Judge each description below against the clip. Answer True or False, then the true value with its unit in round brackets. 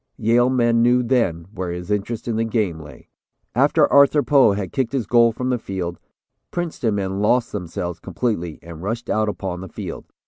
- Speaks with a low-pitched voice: True (110 Hz)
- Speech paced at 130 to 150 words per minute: False (185 wpm)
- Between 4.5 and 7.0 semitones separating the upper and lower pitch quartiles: True (4.9 semitones)